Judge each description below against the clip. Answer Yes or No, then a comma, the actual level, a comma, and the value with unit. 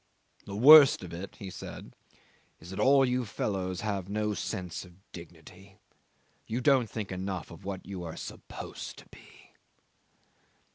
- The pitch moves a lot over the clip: No, average, 3.0 semitones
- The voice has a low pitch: Yes, very low, 95 Hz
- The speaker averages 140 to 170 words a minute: Yes, average, 150 wpm